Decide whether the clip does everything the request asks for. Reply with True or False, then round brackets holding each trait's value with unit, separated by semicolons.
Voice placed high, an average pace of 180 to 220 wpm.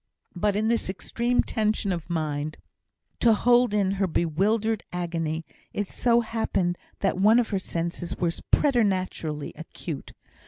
False (195 Hz; 135 wpm)